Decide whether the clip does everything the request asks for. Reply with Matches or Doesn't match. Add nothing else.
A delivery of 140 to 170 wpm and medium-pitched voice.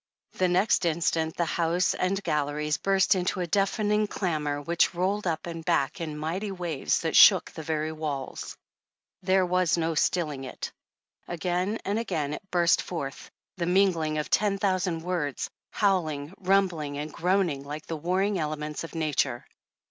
Matches